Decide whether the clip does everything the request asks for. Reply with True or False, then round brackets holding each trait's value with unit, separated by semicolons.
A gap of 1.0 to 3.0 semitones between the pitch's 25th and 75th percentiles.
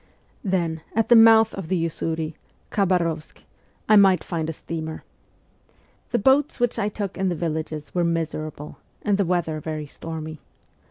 False (3.9 semitones)